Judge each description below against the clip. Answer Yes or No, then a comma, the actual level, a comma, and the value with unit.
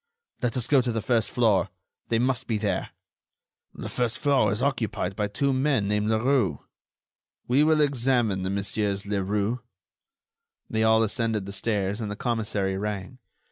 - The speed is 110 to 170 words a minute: Yes, average, 160 wpm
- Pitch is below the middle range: Yes, low, 110 Hz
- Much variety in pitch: No, average, 3.6 semitones